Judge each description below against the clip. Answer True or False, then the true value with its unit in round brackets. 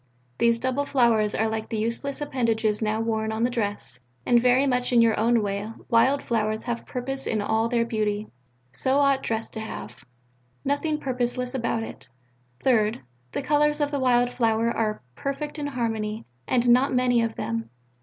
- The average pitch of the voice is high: True (235 Hz)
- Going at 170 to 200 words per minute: True (175 wpm)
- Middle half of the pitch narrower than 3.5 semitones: True (3.0 semitones)